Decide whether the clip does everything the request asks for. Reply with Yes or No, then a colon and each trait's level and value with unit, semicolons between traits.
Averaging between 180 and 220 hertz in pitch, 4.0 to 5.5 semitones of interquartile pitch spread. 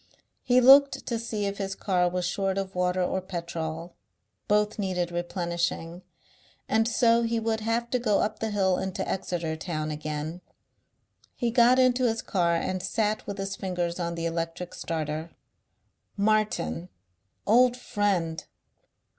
Yes: high, 190 Hz; average, 4.4 semitones